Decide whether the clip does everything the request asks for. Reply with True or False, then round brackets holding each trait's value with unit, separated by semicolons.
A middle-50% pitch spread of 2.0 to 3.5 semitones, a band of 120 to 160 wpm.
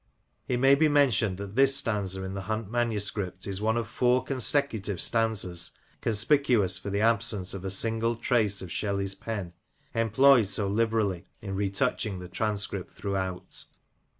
True (3.2 semitones; 150 wpm)